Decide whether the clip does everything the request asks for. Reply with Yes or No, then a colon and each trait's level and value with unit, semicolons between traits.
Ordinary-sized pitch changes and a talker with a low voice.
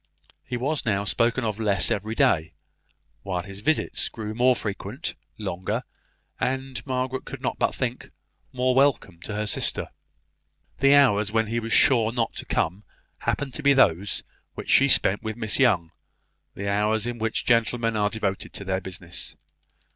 Yes: average, 3.8 semitones; low, 110 Hz